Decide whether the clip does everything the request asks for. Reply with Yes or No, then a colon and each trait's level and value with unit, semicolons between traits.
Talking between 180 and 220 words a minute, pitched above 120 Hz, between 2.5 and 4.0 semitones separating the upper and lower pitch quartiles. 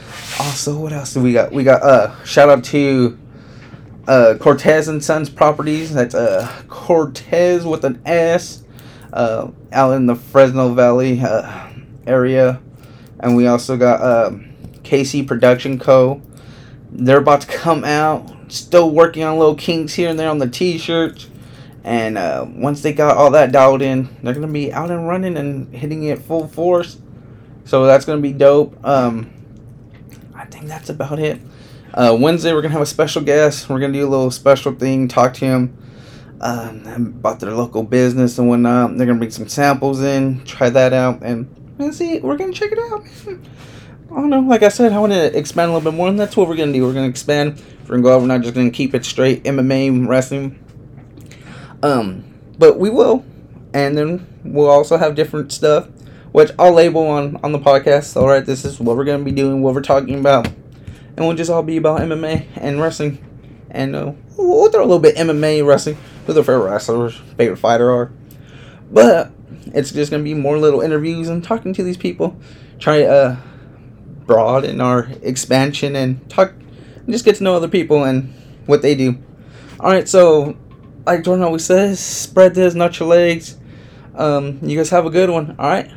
Yes: average, 195 wpm; medium, 140 Hz; average, 3.5 semitones